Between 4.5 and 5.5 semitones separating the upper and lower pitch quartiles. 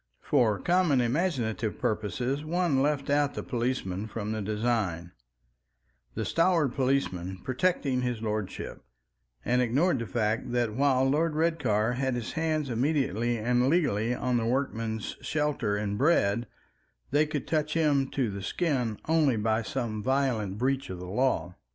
Yes: average, 4.8 semitones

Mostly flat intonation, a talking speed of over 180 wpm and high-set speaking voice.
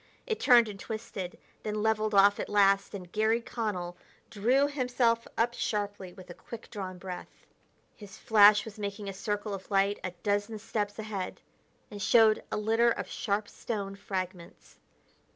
No: narrow, 2.0 semitones; average, 160 wpm; high, 205 Hz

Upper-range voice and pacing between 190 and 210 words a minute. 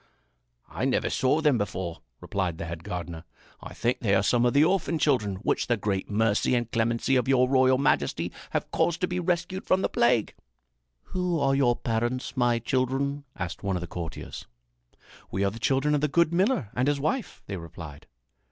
No: low, 125 Hz; average, 195 wpm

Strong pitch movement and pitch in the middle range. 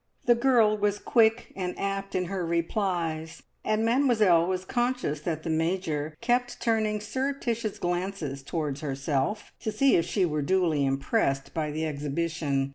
Yes: wide, 5.8 semitones; medium, 180 Hz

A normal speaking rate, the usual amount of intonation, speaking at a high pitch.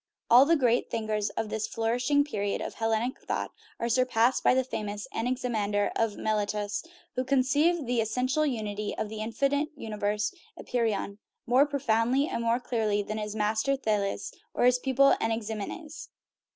Yes: average, 155 wpm; average, 3.3 semitones; high, 230 Hz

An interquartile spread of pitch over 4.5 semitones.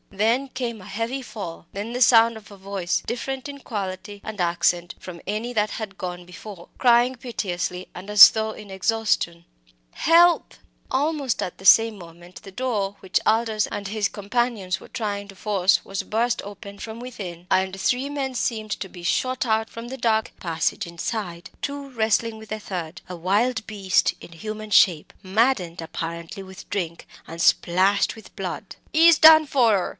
No: average, 4.0 semitones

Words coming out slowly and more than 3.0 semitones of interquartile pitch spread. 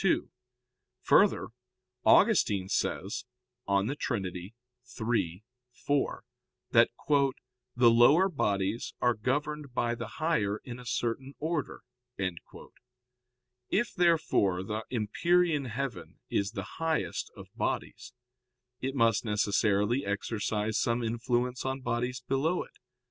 Yes: slow, 105 wpm; average, 4.5 semitones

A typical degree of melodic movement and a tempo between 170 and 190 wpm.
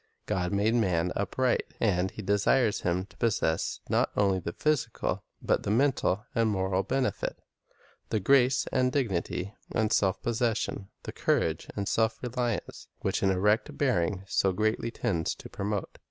No: average, 3.9 semitones; average, 155 wpm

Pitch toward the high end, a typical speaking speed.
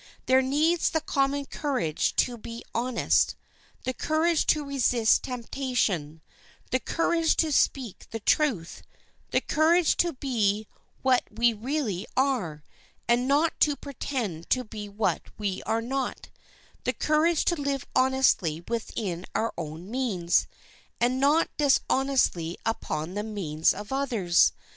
No: very high, 250 Hz; slow, 130 wpm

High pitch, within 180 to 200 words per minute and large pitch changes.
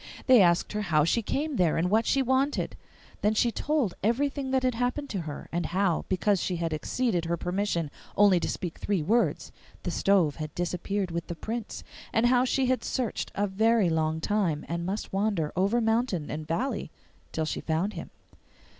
Yes: high, 200 Hz; average, 190 wpm; wide, 5.7 semitones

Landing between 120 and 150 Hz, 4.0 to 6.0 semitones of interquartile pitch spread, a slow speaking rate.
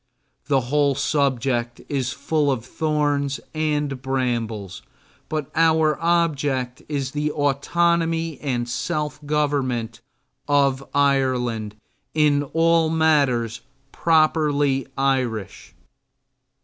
No: medium, 140 Hz; average, 2.9 semitones; slow, 90 wpm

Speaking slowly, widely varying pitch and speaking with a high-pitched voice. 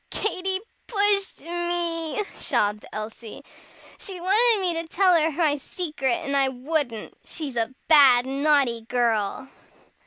Yes: slow, 125 wpm; wide, 5.8 semitones; very high, 310 Hz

